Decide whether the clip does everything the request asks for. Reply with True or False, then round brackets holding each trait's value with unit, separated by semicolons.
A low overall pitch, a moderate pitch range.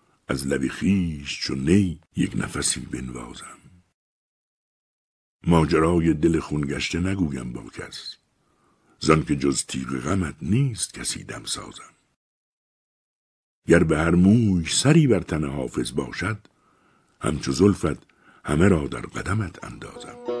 True (80 Hz; 4.8 semitones)